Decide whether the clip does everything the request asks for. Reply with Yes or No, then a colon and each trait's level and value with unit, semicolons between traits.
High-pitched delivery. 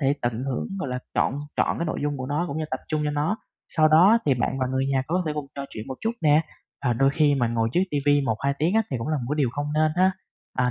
No: medium, 145 Hz